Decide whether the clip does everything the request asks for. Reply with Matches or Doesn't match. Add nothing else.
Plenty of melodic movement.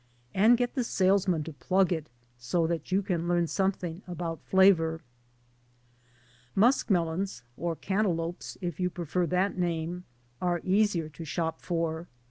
Doesn't match